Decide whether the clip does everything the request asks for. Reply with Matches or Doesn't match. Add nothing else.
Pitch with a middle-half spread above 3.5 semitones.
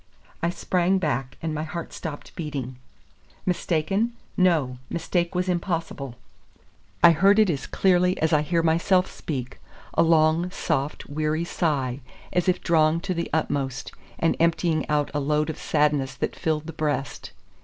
Doesn't match